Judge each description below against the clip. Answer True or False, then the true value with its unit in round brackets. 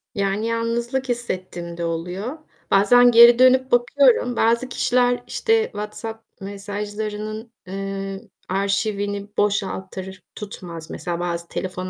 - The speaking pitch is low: False (210 Hz)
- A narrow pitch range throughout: False (3.7 semitones)